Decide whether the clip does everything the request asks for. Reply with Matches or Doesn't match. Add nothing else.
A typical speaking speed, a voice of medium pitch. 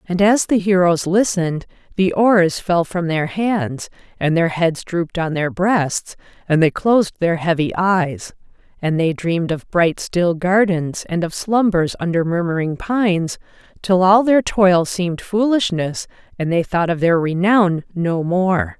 Matches